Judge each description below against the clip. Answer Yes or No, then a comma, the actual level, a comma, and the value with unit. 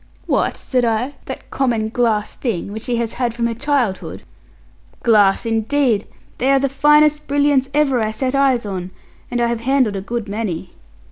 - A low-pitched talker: No, high, 235 Hz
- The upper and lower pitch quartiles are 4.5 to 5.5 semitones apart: No, average, 3.8 semitones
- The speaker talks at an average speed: Yes, average, 180 wpm